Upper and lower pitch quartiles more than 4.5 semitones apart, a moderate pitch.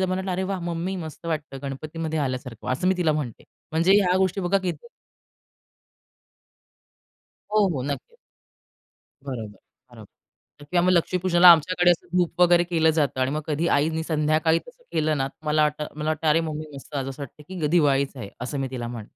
No: average, 4.0 semitones; medium, 155 Hz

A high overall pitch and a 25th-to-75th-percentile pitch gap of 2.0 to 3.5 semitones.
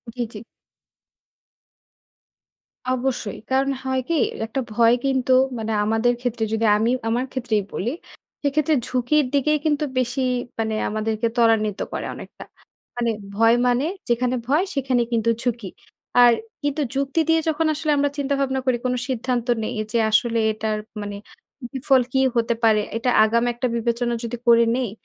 Yes: high, 245 Hz; average, 2.8 semitones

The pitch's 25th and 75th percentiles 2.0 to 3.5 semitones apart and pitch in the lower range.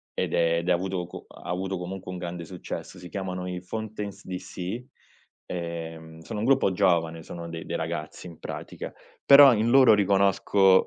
Yes: average, 2.7 semitones; very low, 90 Hz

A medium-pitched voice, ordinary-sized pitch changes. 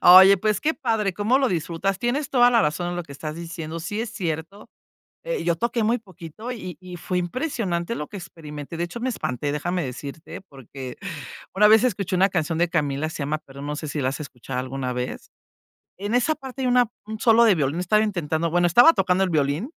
No: medium, 175 Hz; wide, 6.0 semitones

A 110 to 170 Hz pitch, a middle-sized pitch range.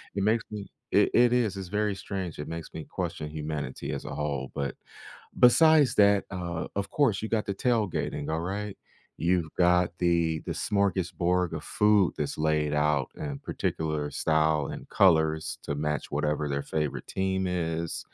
No: very low, 85 Hz; average, 4.6 semitones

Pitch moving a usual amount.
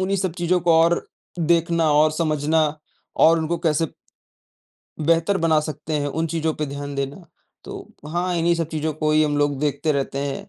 No: narrow, 1.9 semitones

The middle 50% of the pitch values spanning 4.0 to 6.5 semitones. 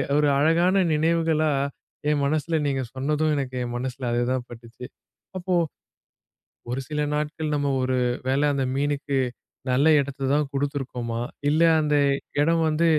No: average, 2.9 semitones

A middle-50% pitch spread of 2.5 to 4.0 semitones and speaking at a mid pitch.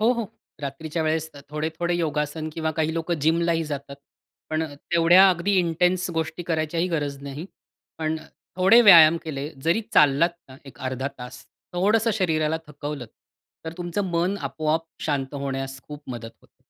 Yes: average, 2.8 semitones; medium, 160 Hz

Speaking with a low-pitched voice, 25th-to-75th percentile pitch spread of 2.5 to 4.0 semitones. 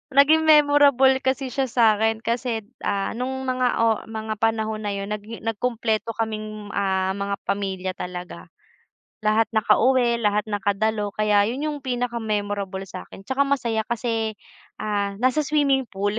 No: high, 220 Hz; average, 3.5 semitones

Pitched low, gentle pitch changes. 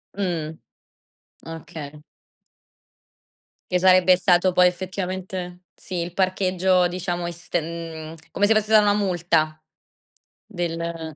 No: medium, 180 Hz; narrow, 2.0 semitones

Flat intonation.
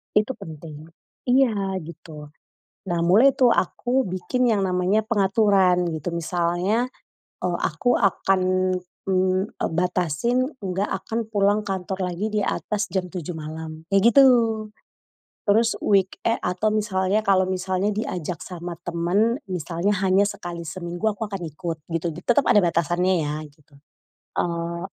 No: average, 3.4 semitones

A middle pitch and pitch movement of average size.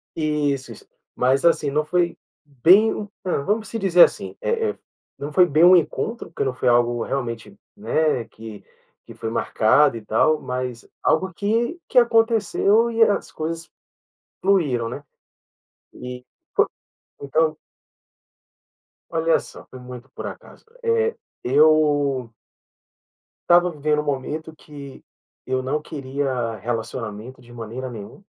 No: medium, 150 Hz; wide, 6.0 semitones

